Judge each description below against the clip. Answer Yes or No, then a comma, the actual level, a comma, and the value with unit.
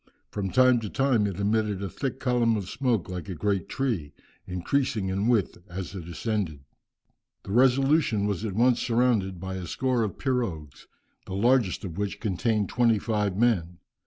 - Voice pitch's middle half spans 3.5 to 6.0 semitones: Yes, average, 4.4 semitones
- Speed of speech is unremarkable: Yes, average, 170 wpm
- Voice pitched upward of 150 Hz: No, low, 105 Hz